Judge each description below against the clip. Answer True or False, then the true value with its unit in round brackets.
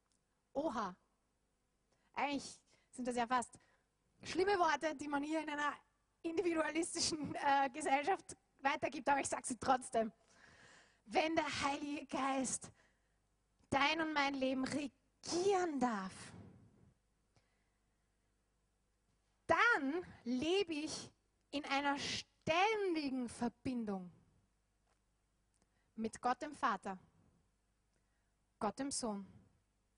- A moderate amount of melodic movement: False (6.6 semitones)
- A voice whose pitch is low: False (270 Hz)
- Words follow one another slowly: True (90 wpm)